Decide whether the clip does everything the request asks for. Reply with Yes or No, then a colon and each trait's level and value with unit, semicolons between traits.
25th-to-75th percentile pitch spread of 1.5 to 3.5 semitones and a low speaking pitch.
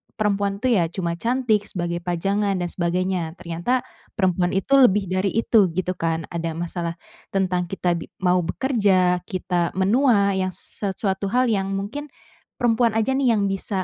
No: average, 3.1 semitones; high, 190 Hz